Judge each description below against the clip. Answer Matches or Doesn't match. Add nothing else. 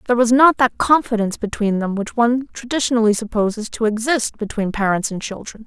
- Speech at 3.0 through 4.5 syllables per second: Doesn't match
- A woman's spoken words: Matches